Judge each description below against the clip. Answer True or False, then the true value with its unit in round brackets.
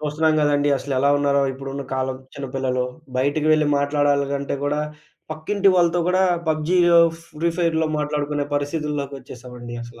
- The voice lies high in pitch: False (145 Hz)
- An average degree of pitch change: False (2.2 semitones)